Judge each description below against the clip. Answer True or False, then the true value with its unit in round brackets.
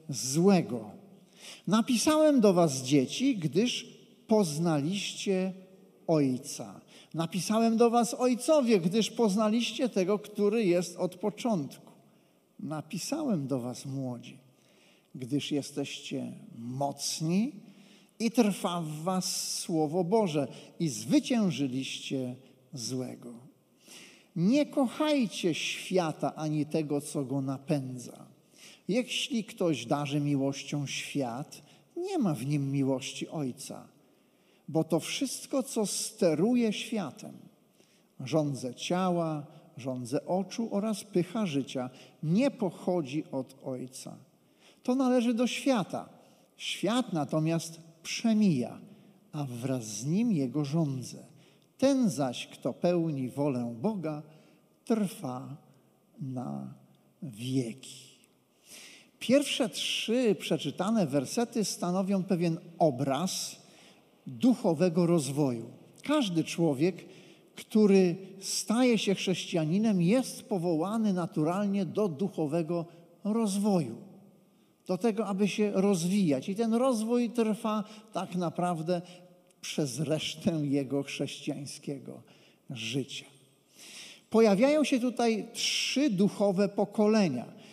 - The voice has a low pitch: False (180 Hz)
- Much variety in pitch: True (6.6 semitones)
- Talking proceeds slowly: True (95 wpm)